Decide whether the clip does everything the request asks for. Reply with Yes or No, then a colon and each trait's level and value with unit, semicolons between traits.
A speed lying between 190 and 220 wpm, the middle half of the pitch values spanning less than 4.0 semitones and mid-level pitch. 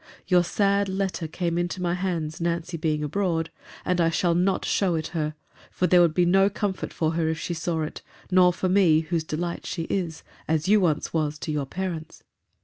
Yes: average, 200 wpm; narrow, 2.5 semitones; medium, 170 Hz